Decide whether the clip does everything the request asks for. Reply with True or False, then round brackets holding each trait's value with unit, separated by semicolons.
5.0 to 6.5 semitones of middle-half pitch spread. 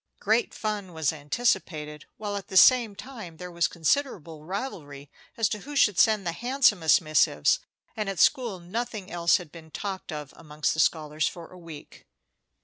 True (5.3 semitones)